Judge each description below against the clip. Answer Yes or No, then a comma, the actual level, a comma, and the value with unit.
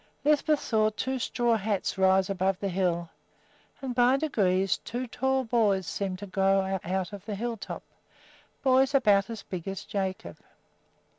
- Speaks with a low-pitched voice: No, high, 200 Hz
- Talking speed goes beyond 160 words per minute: No, average, 155 wpm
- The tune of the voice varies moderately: Yes, average, 4.2 semitones